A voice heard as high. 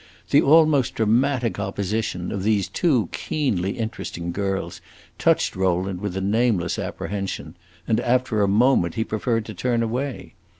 No: low, 110 Hz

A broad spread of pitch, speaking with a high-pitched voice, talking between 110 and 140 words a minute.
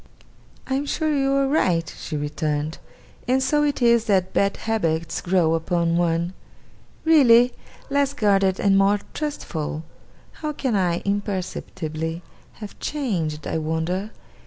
Yes: wide, 7.8 semitones; high, 195 Hz; slow, 135 wpm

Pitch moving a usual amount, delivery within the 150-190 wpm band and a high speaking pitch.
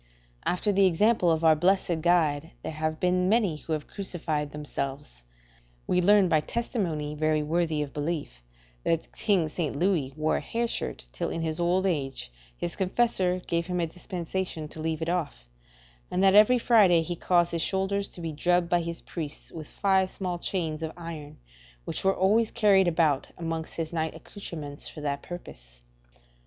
No: average, 3.2 semitones; average, 175 wpm; medium, 170 Hz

